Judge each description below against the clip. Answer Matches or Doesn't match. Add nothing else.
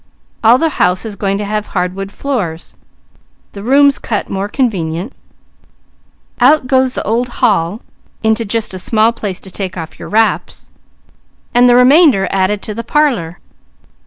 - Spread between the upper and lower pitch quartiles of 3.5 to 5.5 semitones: Matches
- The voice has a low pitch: Doesn't match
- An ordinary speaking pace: Matches